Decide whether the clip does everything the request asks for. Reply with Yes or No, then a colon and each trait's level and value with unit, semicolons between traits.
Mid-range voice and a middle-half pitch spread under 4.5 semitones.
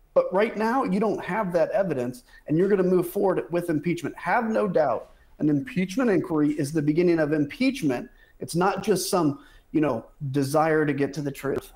No: medium, 170 Hz; average, 5.0 semitones